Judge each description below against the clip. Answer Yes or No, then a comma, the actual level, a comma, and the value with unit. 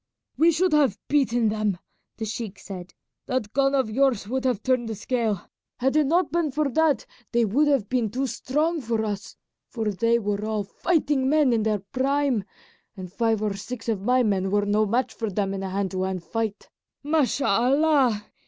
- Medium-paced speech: Yes, average, 190 wpm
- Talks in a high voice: Yes, high, 230 Hz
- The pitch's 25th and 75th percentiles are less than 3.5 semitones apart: No, average, 4.8 semitones